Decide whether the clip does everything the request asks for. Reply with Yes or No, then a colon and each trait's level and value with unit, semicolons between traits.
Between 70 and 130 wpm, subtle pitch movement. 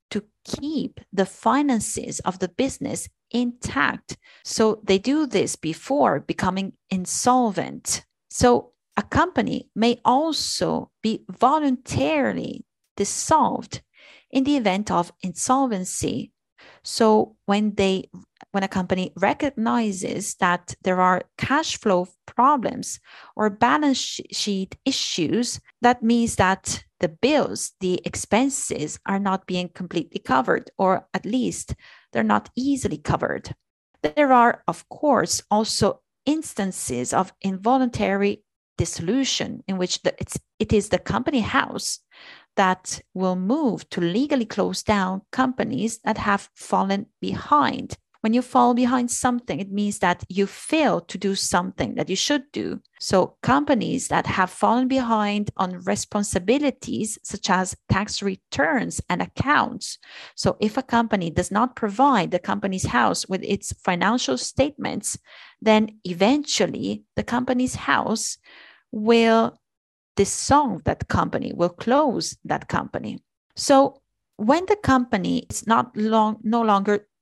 No: average, 125 wpm; average, 4.8 semitones